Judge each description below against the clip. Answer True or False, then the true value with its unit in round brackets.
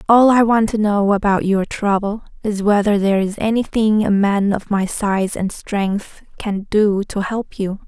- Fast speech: False (190 wpm)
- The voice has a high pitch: True (205 Hz)